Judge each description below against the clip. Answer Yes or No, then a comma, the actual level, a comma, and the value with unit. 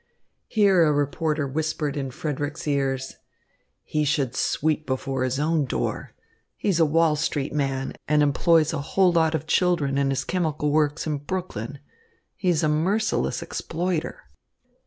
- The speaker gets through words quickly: No, average, 150 wpm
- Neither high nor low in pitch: Yes, medium, 150 Hz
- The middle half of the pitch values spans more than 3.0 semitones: No, average, 2.7 semitones